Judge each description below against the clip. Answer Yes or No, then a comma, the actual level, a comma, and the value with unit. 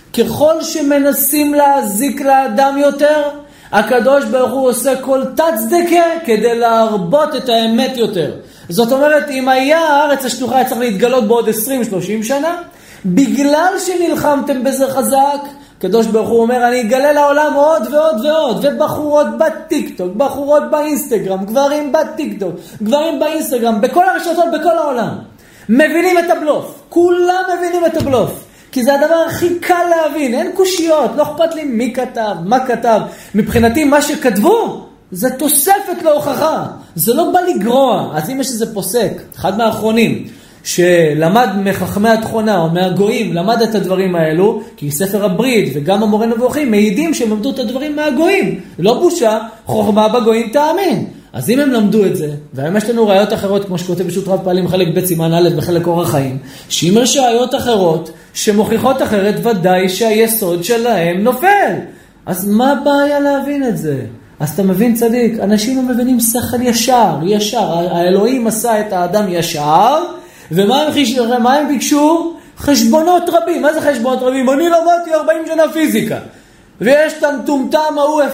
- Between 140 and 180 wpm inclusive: Yes, average, 145 wpm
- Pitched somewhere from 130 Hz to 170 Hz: No, very high, 255 Hz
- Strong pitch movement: Yes, wide, 5.8 semitones